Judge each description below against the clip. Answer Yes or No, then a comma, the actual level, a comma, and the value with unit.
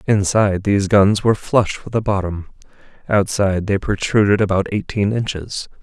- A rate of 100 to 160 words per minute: Yes, average, 145 wpm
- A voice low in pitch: Yes, low, 100 Hz